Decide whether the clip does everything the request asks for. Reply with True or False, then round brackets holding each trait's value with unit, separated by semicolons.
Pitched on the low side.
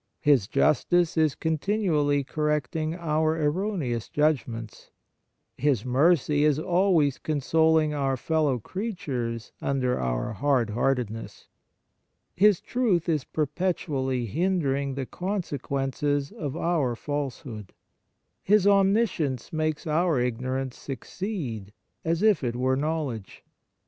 False (150 Hz)